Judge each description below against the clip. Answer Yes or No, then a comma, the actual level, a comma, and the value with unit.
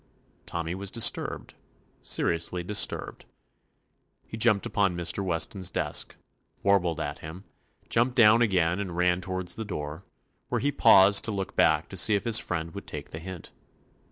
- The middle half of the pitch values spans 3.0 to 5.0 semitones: Yes, average, 3.4 semitones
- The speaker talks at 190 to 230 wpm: No, average, 165 wpm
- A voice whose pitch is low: Yes, very low, 95 Hz